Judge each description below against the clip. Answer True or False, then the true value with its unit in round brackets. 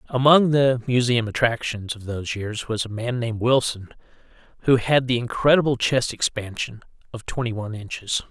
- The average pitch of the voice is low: True (120 Hz)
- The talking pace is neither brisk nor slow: True (160 wpm)